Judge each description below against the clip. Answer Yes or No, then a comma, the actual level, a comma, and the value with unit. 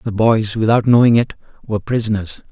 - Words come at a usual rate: Yes, average, 165 wpm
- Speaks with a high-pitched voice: No, low, 110 Hz